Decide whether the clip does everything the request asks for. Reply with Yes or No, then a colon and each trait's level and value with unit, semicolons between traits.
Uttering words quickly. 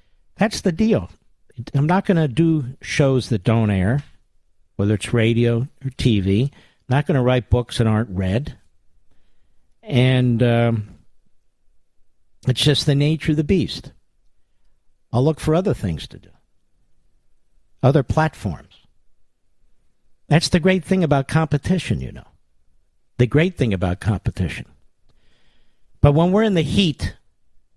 No: slow, 135 wpm